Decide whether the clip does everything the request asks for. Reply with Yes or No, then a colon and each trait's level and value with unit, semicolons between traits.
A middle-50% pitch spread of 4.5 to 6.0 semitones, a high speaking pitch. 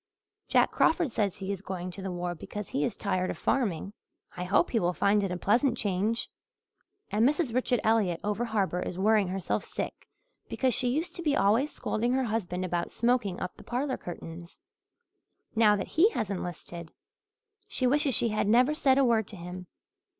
Yes: average, 5.3 semitones; high, 210 Hz